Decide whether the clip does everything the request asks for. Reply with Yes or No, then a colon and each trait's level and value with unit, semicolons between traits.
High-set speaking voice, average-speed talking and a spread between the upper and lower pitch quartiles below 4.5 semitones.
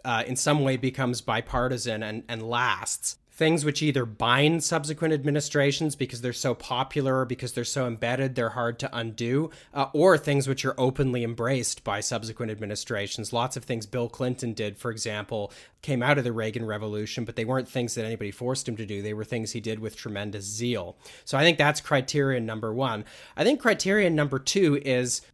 No: low, 125 Hz; average, 195 wpm; average, 3.3 semitones